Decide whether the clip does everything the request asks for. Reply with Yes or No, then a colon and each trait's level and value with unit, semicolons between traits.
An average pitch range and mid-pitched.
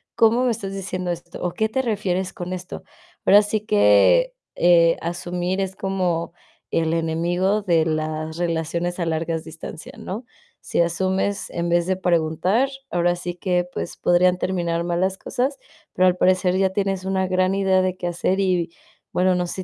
No: narrow, 1.9 semitones; medium, 180 Hz